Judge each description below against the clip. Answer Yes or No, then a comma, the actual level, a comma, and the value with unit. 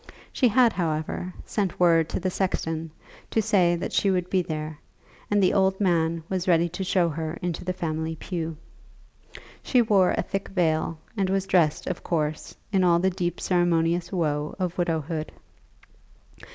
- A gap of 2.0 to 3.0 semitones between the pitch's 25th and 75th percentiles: Yes, average, 2.7 semitones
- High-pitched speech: No, medium, 175 Hz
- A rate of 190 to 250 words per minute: No, average, 165 wpm